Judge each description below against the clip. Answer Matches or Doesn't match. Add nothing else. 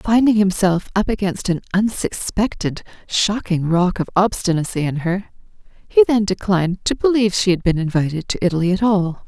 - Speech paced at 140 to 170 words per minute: Matches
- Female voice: Matches